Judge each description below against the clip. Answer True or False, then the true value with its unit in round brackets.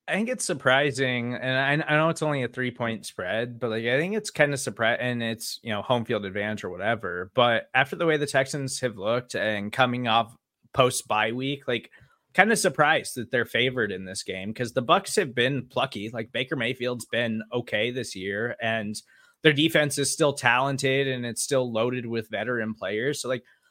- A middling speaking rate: False (210 wpm)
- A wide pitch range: False (3.4 semitones)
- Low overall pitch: True (125 Hz)